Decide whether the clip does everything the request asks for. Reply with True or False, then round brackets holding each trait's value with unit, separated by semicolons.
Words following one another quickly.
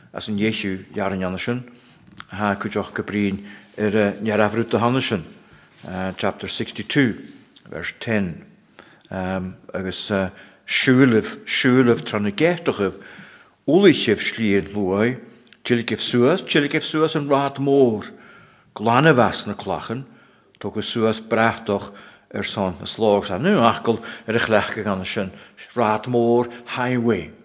False (135 wpm)